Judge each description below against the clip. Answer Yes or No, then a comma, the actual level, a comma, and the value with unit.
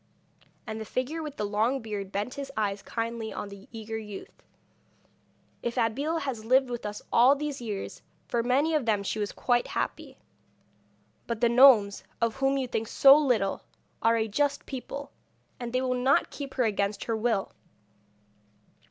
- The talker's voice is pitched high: Yes, high, 235 Hz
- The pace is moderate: Yes, average, 170 wpm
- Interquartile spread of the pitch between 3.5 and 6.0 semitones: Yes, average, 3.8 semitones